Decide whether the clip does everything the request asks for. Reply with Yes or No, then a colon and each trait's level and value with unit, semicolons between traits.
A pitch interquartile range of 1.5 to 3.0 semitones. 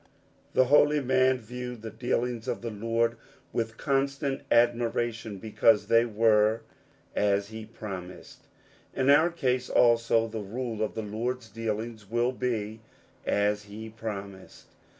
Yes: narrow, 2.5 semitones